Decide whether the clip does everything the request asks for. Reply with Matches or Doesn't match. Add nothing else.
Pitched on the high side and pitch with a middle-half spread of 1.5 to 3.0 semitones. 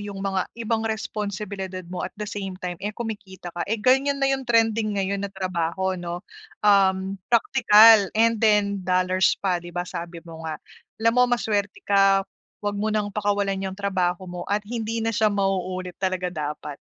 Matches